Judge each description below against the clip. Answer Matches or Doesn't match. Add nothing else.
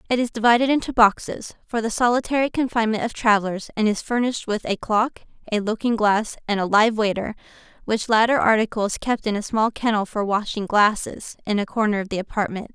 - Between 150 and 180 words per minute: Doesn't match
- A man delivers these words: Doesn't match